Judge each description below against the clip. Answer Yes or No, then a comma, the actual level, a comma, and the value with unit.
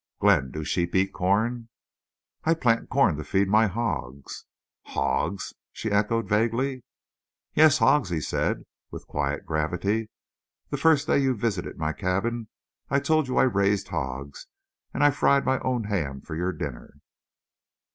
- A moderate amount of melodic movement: No, wide, 6.7 semitones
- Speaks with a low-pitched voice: Yes, low, 105 Hz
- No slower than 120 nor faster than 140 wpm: No, average, 150 wpm